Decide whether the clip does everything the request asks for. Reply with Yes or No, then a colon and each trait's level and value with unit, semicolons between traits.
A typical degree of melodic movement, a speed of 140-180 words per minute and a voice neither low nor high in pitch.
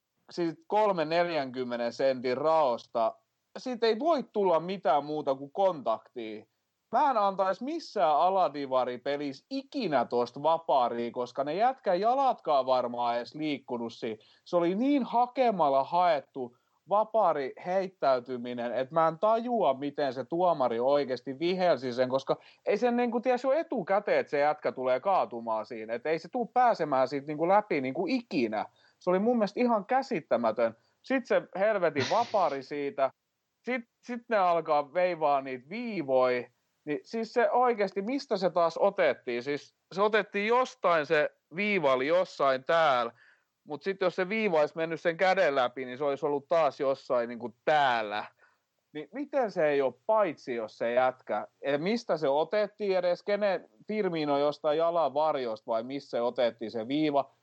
No: wide, 7.7 semitones; fast, 155 wpm; medium, 160 Hz